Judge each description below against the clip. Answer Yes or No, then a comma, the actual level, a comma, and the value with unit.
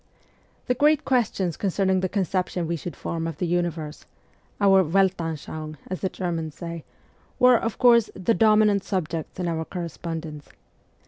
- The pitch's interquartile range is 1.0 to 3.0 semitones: No, average, 3.4 semitones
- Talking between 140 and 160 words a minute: Yes, average, 145 wpm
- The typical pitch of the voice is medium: Yes, medium, 180 Hz